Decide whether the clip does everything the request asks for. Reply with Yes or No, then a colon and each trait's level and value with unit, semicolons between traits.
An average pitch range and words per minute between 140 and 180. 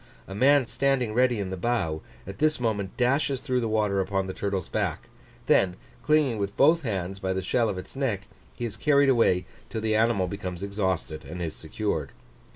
No: average, 5.0 semitones; average, 195 wpm